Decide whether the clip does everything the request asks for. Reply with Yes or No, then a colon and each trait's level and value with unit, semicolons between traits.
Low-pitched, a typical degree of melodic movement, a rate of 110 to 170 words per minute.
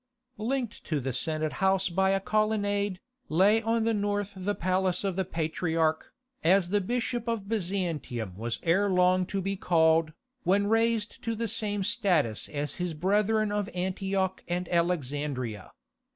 No: high, 190 Hz; average, 3.8 semitones; average, 150 wpm